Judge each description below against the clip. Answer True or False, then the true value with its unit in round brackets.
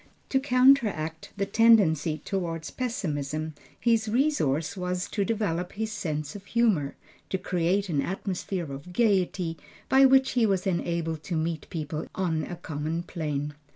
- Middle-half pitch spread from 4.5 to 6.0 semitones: True (5.5 semitones)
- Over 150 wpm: False (145 wpm)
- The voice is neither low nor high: True (180 Hz)